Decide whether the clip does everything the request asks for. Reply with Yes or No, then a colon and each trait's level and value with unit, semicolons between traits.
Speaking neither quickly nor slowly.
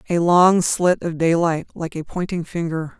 Yes: average, 180 wpm